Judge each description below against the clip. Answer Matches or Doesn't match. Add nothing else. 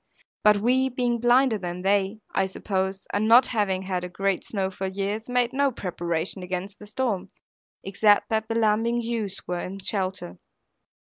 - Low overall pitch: Doesn't match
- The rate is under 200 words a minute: Matches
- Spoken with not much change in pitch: Doesn't match